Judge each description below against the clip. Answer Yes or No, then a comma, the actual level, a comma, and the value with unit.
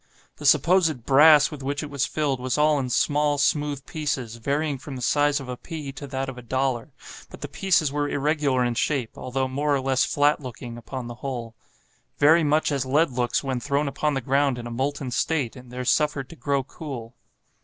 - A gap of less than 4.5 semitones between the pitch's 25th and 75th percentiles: Yes, narrow, 2.6 semitones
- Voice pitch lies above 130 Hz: Yes, medium, 140 Hz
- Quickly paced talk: Yes, fast, 210 wpm